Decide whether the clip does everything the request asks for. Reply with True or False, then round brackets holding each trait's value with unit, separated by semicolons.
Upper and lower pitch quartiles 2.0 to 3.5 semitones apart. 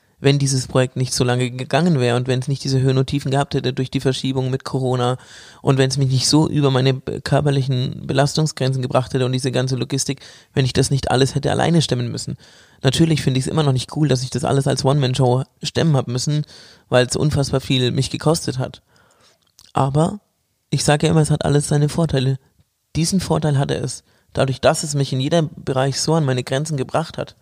True (2.4 semitones)